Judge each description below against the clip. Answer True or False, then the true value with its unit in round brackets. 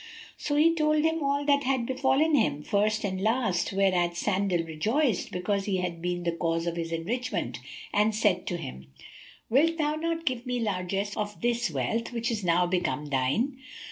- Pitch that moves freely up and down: True (6.8 semitones)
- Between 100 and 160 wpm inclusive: False (180 wpm)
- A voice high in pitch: True (210 Hz)